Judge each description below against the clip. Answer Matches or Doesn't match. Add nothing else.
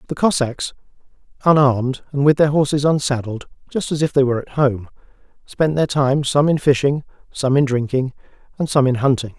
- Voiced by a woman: Doesn't match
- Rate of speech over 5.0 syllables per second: Matches